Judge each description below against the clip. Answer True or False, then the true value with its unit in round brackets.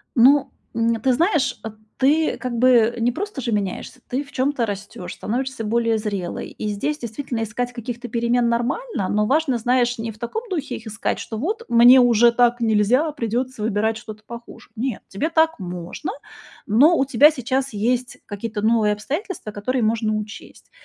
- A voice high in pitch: True (235 Hz)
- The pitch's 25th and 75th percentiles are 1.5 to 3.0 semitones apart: False (3.4 semitones)